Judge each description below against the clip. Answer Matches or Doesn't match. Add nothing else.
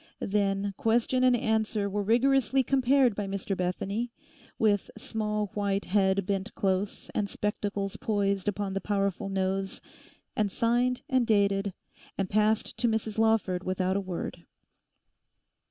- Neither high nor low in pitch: Doesn't match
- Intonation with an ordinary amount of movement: Doesn't match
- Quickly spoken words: Doesn't match